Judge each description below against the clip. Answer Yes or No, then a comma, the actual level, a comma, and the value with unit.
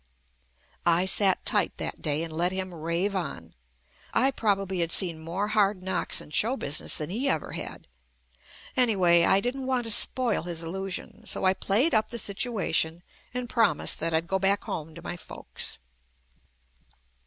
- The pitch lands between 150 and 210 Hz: Yes, high, 190 Hz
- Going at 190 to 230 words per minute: No, average, 165 wpm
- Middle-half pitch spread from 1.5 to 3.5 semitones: No, average, 4.6 semitones